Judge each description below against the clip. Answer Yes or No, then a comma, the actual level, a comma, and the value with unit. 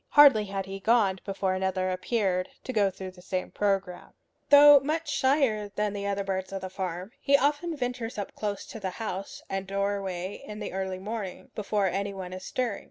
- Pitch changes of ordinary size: Yes, average, 3.1 semitones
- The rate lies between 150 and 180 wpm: No, average, 190 wpm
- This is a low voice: No, high, 200 Hz